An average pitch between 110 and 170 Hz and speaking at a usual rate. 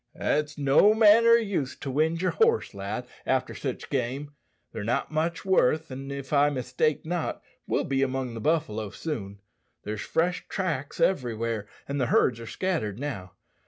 Yes: medium, 140 Hz; average, 165 wpm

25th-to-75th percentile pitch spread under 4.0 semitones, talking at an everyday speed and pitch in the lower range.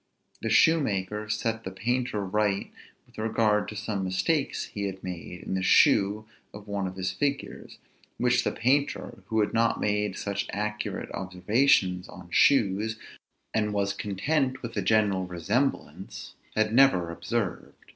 Yes: average, 3.2 semitones; average, 145 wpm; low, 105 Hz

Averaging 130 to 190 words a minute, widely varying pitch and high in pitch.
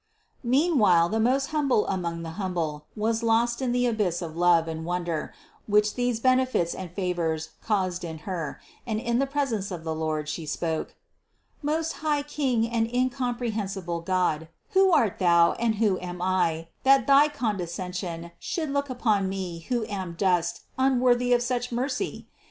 Yes: average, 160 wpm; wide, 6.4 semitones; high, 210 Hz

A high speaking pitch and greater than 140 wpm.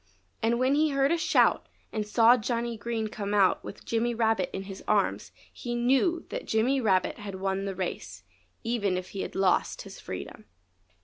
Yes: high, 225 Hz; average, 185 wpm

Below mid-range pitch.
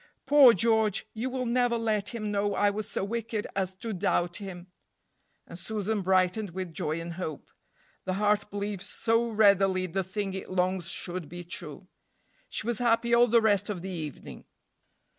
No: high, 200 Hz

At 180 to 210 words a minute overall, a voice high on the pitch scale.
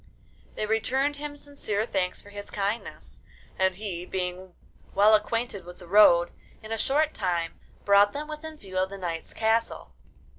No: average, 160 wpm; high, 205 Hz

